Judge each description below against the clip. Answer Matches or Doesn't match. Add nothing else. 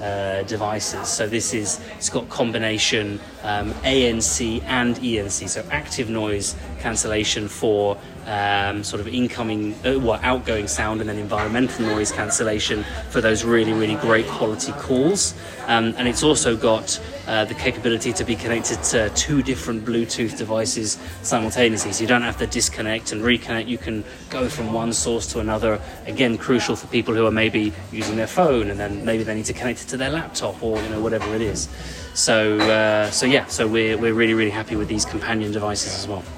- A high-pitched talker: Doesn't match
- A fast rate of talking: Matches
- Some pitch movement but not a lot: Doesn't match